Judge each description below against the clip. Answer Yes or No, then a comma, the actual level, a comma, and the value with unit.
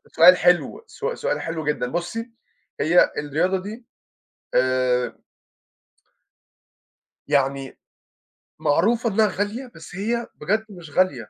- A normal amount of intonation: No, wide, 7.1 semitones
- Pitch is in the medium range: Yes, medium, 180 Hz